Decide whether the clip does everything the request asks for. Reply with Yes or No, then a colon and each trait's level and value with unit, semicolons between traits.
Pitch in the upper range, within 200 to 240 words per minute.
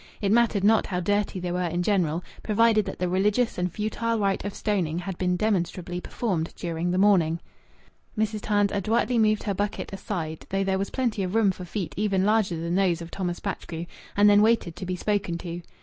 Yes: high, 195 Hz; fast, 205 wpm